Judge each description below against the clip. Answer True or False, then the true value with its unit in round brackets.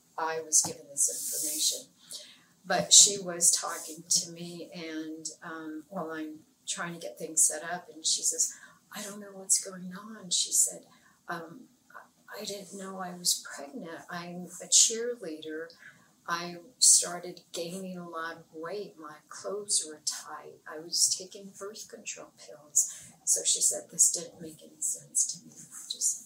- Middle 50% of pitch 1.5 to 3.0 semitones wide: False (3.5 semitones)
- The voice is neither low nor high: True (175 Hz)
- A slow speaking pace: False (160 wpm)